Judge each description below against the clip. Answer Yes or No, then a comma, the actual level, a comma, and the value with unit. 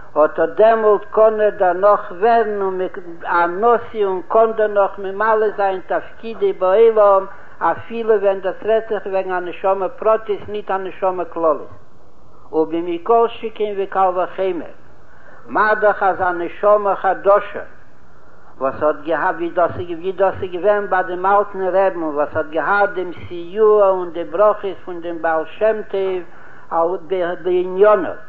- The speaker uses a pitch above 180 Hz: Yes, high, 190 Hz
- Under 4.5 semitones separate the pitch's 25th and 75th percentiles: Yes, average, 3.1 semitones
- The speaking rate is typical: Yes, average, 130 wpm